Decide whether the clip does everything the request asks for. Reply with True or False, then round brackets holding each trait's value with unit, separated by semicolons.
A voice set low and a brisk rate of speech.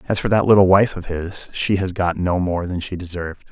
True (90 Hz; 255 wpm)